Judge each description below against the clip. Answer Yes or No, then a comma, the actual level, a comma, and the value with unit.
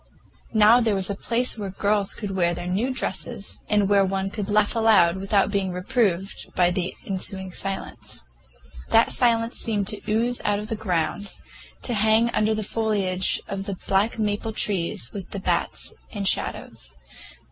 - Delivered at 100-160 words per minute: No, average, 170 wpm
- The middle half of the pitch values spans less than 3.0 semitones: Yes, narrow, 2.4 semitones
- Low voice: No, high, 205 Hz